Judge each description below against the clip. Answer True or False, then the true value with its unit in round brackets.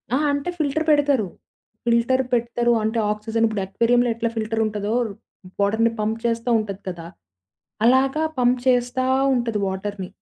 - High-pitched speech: True (230 Hz)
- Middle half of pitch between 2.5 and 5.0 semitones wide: True (2.8 semitones)